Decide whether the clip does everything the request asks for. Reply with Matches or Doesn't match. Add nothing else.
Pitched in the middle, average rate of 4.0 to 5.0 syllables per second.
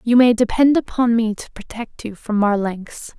Doesn't match